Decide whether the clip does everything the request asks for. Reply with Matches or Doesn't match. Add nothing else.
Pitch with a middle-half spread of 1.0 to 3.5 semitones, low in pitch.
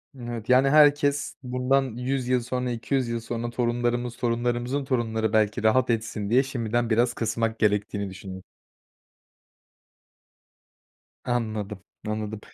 Matches